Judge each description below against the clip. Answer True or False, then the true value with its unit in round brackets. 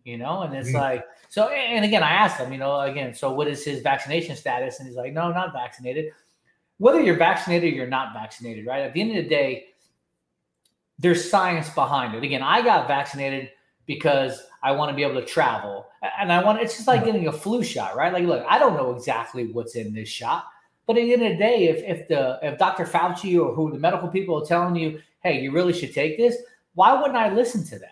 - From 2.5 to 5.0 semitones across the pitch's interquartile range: False (5.5 semitones)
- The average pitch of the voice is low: False (160 Hz)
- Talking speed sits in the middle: False (240 wpm)